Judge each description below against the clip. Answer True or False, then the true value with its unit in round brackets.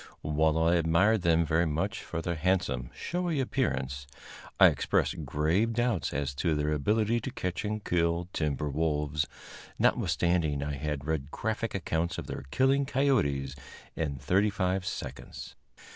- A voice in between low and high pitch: False (85 Hz)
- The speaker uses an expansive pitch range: True (5.7 semitones)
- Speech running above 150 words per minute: False (145 wpm)